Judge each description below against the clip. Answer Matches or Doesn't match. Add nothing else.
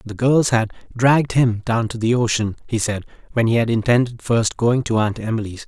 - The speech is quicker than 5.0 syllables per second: Matches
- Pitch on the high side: Doesn't match